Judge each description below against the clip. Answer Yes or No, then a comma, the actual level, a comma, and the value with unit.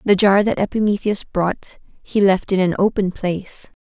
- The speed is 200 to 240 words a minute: No, average, 175 wpm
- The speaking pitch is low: No, high, 195 Hz